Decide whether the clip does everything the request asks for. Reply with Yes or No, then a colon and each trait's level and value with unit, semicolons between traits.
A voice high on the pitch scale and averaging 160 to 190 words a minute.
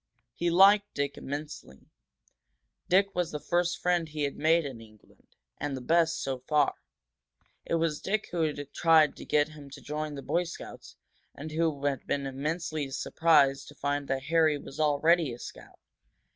No: medium, 150 Hz; average, 170 wpm